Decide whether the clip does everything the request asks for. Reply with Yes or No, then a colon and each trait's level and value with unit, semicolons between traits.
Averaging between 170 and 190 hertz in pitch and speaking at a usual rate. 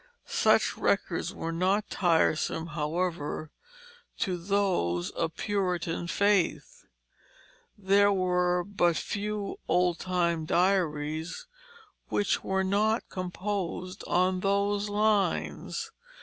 No: medium, 185 Hz; slow, 90 wpm